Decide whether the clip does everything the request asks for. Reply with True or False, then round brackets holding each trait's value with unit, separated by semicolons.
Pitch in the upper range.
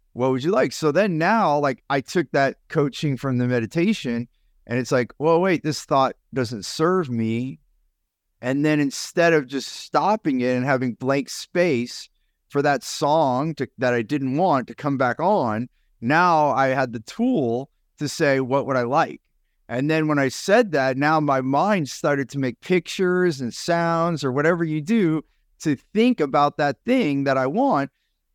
False (140 Hz)